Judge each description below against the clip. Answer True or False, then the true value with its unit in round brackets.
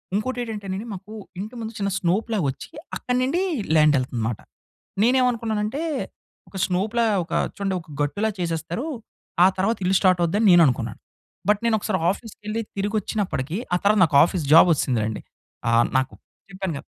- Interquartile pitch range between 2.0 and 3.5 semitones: False (5.0 semitones)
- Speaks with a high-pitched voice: True (195 Hz)